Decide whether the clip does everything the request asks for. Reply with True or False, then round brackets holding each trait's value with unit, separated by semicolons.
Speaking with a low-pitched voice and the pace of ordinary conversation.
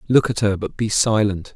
False (105 Hz; 230 wpm)